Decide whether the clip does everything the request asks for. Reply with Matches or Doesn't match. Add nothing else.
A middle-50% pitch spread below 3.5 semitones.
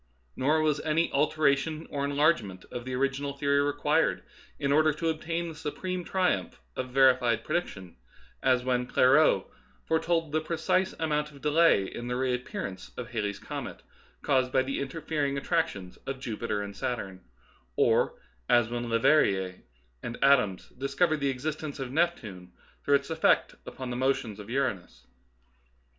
Doesn't match